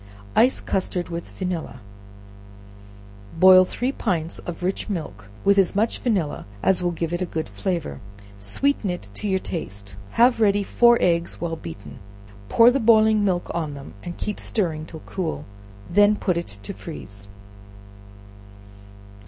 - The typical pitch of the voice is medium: Yes, medium, 180 Hz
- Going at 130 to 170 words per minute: Yes, average, 150 wpm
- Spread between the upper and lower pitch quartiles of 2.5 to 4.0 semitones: No, average, 4.4 semitones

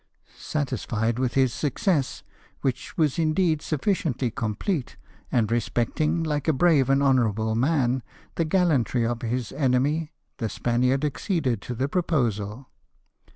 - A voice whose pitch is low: Yes, low, 130 Hz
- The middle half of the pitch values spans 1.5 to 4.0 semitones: No, average, 4.5 semitones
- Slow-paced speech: Yes, slow, 125 wpm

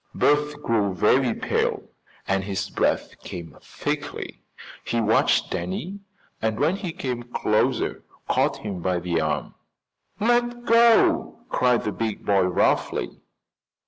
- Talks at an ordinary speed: No, slow, 125 wpm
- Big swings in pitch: Yes, wide, 7.7 semitones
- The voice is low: Yes, low, 115 Hz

